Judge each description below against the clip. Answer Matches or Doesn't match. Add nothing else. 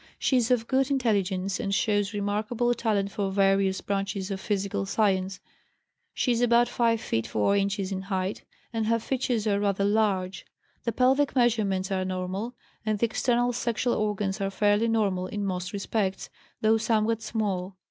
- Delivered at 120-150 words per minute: Doesn't match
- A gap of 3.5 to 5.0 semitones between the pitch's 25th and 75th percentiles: Doesn't match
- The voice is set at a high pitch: Matches